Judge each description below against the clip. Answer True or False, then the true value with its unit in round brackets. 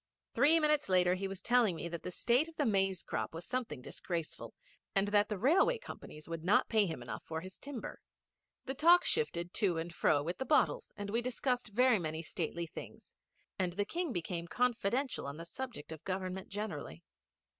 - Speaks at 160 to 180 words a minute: False (195 wpm)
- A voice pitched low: False (195 Hz)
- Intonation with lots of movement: True (6.6 semitones)